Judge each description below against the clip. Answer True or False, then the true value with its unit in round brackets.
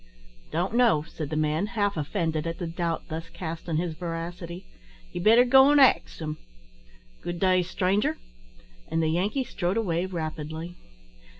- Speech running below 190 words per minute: True (160 wpm)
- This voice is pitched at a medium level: True (175 Hz)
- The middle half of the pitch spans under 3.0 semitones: False (3.3 semitones)